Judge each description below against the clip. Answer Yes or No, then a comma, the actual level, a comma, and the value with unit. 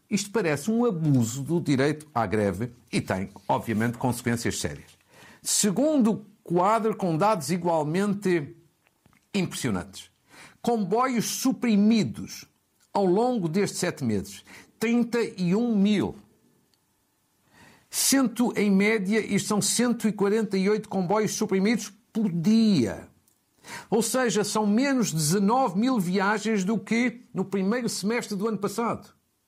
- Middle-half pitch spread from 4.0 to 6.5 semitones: Yes, average, 4.6 semitones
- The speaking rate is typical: No, slow, 110 wpm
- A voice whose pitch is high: Yes, high, 205 Hz